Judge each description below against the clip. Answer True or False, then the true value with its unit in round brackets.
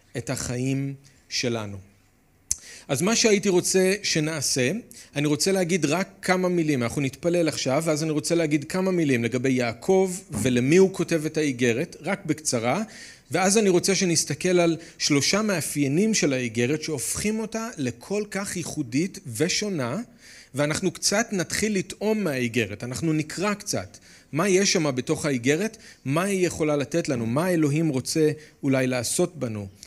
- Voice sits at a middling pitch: True (155 Hz)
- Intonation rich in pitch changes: True (6.0 semitones)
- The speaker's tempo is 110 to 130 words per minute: False (145 wpm)